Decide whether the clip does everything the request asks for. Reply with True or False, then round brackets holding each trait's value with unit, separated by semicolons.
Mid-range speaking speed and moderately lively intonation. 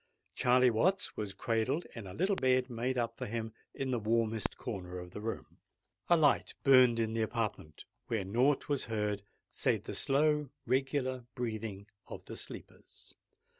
True (165 wpm; 3.3 semitones)